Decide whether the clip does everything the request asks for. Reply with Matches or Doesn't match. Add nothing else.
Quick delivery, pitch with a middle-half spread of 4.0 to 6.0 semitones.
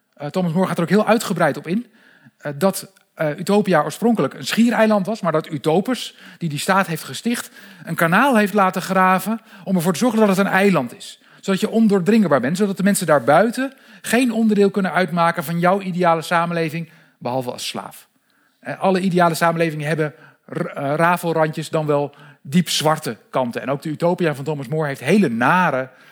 Doesn't match